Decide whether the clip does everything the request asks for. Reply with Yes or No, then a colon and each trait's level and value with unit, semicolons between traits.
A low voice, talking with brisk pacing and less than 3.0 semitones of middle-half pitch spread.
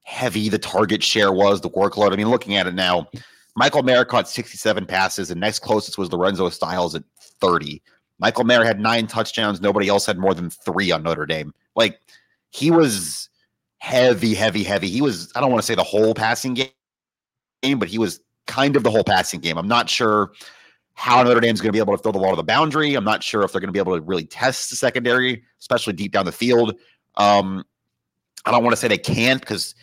No: low, 105 Hz; fast, 220 wpm; average, 3.3 semitones